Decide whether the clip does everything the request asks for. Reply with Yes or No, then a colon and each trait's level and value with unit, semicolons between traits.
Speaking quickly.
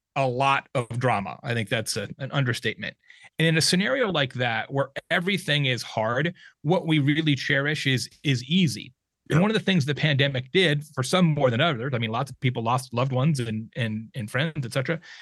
Yes: fast, 215 wpm